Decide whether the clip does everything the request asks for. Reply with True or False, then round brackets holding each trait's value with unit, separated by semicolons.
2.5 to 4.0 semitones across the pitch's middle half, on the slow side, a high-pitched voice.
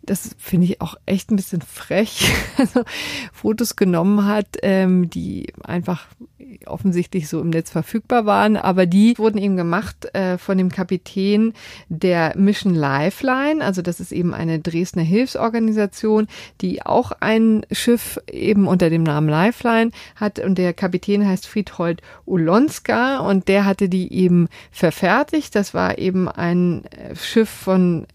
False (3.4 semitones; 140 wpm; 195 Hz)